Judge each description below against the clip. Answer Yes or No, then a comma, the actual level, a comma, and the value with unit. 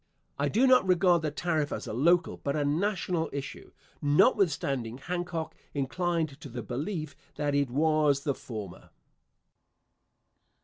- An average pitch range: Yes, average, 3.9 semitones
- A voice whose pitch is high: No, medium, 150 Hz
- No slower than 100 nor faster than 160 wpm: Yes, slow, 135 wpm